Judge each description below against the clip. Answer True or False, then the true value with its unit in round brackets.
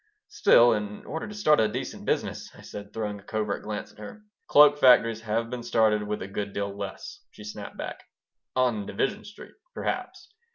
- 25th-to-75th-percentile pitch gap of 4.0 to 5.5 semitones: False (3.4 semitones)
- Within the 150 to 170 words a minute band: False (195 wpm)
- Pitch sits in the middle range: False (110 Hz)